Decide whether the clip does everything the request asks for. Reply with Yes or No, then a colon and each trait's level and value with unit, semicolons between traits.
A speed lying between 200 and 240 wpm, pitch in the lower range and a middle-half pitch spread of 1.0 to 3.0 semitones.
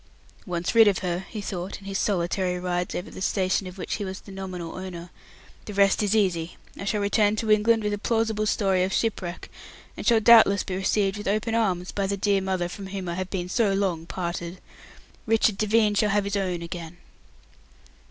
No: fast, 205 wpm; high, 195 Hz; narrow, 2.5 semitones